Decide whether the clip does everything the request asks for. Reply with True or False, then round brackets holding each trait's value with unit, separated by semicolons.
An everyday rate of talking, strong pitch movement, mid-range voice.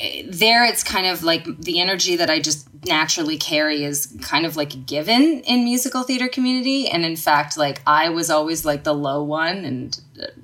True (190 wpm; 6.3 semitones; 160 Hz)